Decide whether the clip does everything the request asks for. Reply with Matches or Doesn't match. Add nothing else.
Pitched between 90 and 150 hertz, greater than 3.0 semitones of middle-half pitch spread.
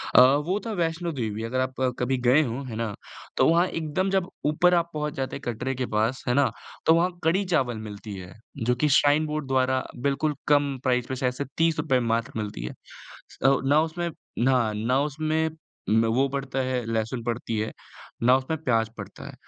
Matches